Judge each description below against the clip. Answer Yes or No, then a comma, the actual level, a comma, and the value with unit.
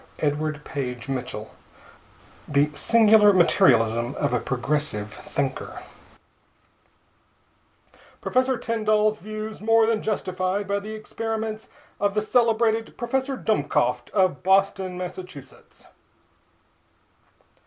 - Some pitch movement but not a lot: No, wide, 7.3 semitones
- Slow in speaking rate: Yes, slow, 90 wpm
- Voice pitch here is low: No, high, 195 Hz